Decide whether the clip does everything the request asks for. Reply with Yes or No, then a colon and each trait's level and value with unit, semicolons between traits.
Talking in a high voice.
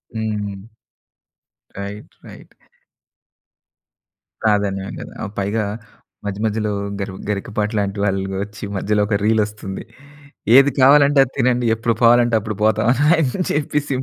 No: low, 105 Hz